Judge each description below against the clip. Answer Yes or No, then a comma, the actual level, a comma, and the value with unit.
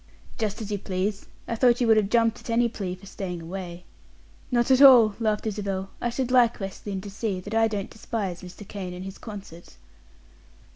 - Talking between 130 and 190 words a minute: No, fast, 205 wpm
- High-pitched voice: Yes, high, 205 Hz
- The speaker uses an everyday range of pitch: Yes, average, 3.2 semitones